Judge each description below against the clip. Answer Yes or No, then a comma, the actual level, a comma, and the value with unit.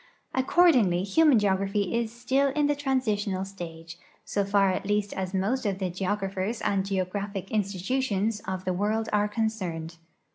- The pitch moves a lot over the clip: No, average, 2.9 semitones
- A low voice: No, high, 200 Hz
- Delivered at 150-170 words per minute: Yes, average, 155 wpm